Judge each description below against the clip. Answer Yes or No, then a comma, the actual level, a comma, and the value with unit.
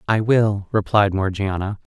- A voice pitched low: Yes, low, 100 Hz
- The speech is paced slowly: Yes, slow, 125 wpm